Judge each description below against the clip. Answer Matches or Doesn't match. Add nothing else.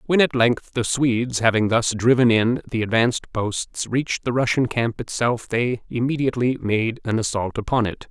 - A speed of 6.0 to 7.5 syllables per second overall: Doesn't match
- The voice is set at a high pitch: Doesn't match